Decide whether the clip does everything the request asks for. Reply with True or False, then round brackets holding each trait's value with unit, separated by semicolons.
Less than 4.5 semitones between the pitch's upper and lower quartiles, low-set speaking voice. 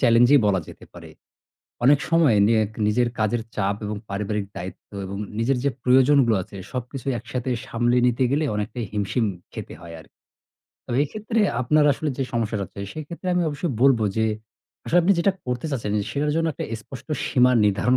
False (5.0 semitones; 125 Hz)